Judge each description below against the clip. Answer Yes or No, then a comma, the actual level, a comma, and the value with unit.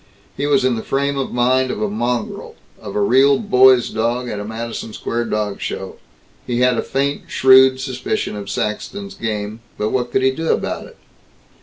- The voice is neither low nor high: No, low, 125 Hz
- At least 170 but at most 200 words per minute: Yes, average, 190 wpm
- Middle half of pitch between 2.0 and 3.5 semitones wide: Yes, average, 3.1 semitones